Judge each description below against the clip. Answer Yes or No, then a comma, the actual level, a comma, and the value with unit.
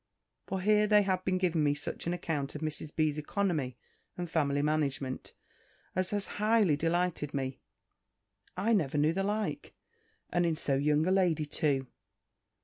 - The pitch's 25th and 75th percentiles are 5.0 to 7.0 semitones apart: No, average, 4.3 semitones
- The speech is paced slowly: No, average, 160 wpm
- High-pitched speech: No, medium, 160 Hz